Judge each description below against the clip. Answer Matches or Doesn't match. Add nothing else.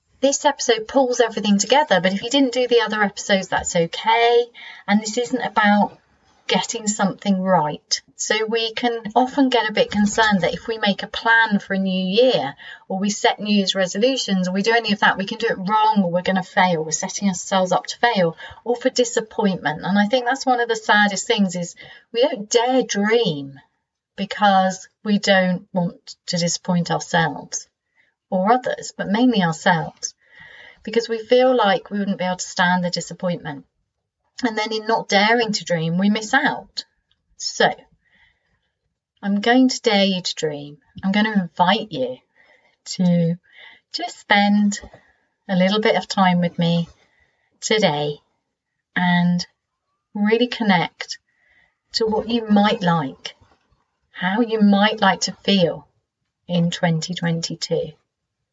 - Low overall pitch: Doesn't match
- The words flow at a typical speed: Matches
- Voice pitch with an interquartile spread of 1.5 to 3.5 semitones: Doesn't match